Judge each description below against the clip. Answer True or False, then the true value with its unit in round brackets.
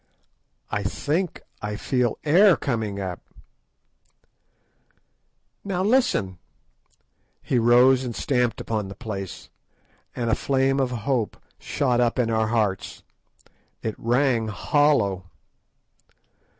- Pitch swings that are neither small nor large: True (4.2 semitones)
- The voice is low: True (120 Hz)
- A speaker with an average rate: False (105 wpm)